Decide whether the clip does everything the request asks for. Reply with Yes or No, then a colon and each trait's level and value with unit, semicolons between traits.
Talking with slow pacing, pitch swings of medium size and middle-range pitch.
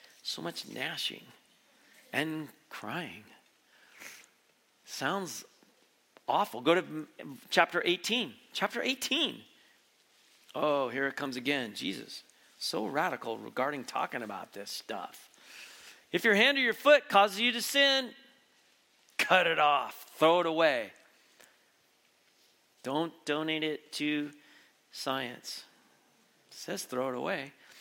No: slow, 110 wpm; wide, 8.1 semitones; medium, 170 Hz